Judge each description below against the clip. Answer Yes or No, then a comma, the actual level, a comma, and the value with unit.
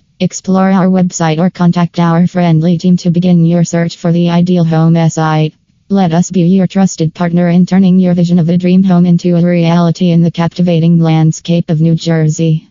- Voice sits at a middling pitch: Yes, medium, 175 Hz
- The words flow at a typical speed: Yes, average, 195 wpm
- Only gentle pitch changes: Yes, narrow, 1.3 semitones